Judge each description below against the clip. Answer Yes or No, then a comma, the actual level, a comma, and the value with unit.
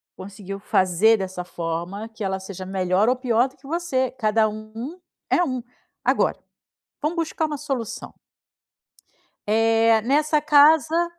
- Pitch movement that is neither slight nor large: No, wide, 6.5 semitones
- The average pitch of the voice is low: No, high, 225 Hz